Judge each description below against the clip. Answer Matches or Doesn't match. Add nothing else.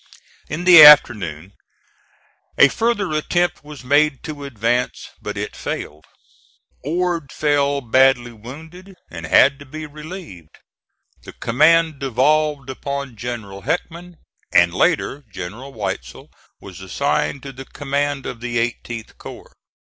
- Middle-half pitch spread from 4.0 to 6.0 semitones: Matches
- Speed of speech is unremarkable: Doesn't match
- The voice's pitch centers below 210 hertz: Matches